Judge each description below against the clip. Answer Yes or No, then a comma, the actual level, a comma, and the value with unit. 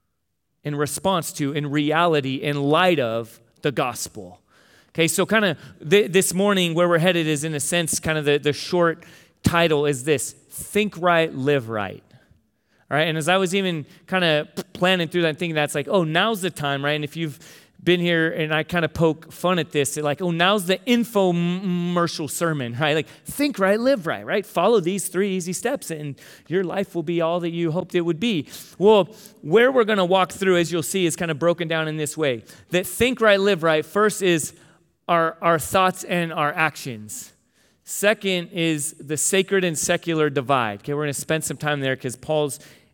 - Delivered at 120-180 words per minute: No, fast, 205 wpm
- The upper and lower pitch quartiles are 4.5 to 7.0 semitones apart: No, average, 3.7 semitones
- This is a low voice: No, medium, 165 Hz